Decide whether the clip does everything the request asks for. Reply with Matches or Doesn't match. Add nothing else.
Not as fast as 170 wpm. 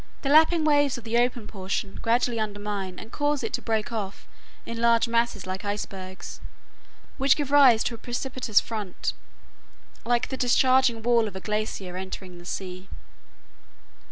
Matches